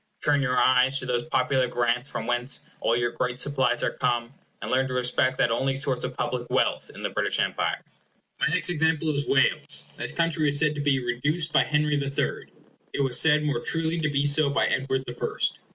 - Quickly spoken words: Yes, fast, 215 wpm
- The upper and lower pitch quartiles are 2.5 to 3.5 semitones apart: Yes, average, 3.1 semitones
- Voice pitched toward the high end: No, low, 135 Hz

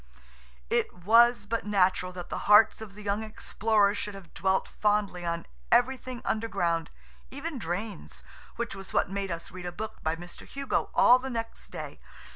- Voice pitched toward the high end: Yes, high, 205 Hz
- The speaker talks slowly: No, average, 170 wpm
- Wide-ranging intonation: No, average, 4.0 semitones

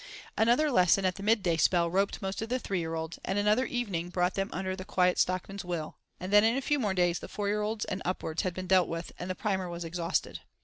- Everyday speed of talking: No, fast, 255 wpm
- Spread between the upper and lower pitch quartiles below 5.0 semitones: Yes, average, 2.8 semitones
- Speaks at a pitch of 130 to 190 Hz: Yes, medium, 185 Hz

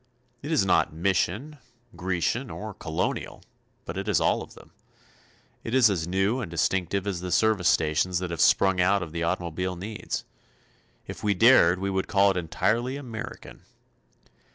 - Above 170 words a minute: No, average, 165 wpm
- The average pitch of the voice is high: No, very low, 95 Hz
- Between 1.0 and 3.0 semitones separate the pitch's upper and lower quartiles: No, average, 3.8 semitones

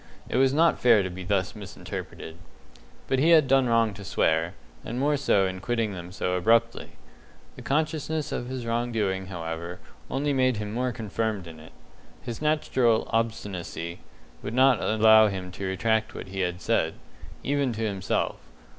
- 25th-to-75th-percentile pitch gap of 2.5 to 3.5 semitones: No, average, 5.2 semitones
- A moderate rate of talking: Yes, average, 170 wpm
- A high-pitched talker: No, low, 110 Hz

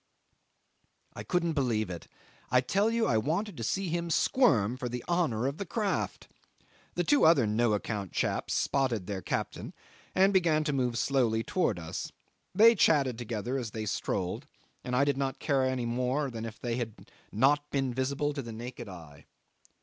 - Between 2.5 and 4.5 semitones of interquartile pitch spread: No, average, 5.2 semitones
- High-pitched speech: No, low, 130 Hz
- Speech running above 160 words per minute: Yes, average, 180 wpm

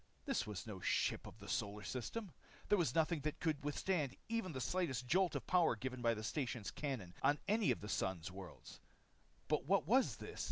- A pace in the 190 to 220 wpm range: Yes, average, 200 wpm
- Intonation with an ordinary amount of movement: No, wide, 8.5 semitones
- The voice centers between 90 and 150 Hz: Yes, medium, 140 Hz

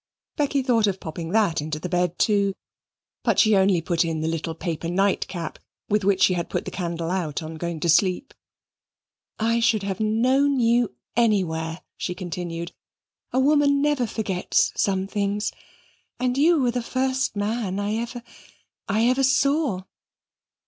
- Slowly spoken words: No, average, 160 wpm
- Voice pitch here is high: Yes, high, 200 Hz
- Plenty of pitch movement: Yes, wide, 5.7 semitones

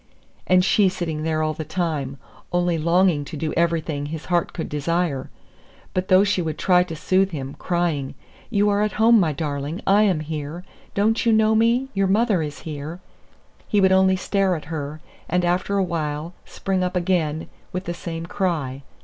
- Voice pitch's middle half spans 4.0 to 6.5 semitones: No, average, 3.5 semitones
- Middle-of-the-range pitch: Yes, medium, 175 Hz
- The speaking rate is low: No, average, 185 wpm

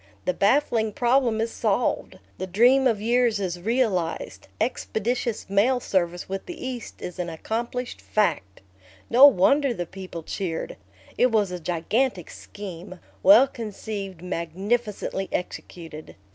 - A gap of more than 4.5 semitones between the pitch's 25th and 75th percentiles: Yes, average, 5.1 semitones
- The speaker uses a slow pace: Yes, slow, 130 wpm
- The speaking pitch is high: Yes, high, 210 Hz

